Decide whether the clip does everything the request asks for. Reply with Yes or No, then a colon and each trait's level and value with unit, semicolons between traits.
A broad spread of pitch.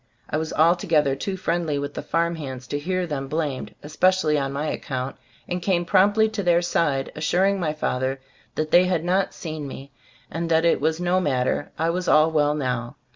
No: average, 3.6 semitones